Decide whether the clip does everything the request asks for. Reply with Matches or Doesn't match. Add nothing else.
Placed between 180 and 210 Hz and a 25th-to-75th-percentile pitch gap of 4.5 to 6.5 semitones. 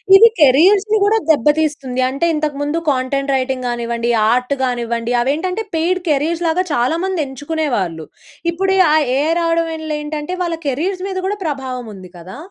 Doesn't match